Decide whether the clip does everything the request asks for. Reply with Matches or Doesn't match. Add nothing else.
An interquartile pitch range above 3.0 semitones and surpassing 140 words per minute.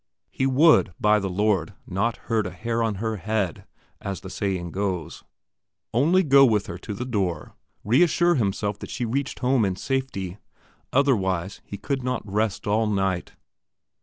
Matches